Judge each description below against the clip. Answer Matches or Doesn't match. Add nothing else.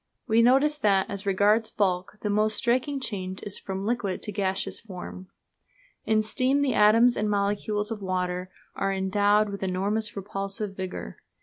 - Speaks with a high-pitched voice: Matches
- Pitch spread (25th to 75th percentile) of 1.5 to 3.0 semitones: Matches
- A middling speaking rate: Matches